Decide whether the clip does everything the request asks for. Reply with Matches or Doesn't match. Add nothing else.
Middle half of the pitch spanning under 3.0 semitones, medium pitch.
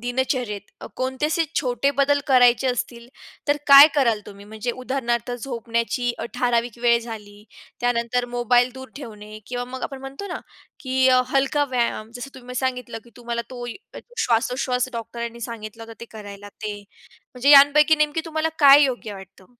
Doesn't match